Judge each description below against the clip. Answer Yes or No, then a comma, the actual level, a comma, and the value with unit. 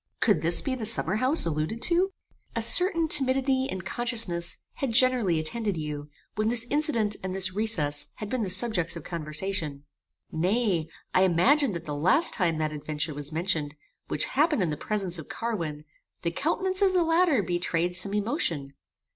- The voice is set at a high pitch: Yes, high, 195 Hz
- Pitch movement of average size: No, wide, 7.7 semitones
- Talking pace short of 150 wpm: No, average, 170 wpm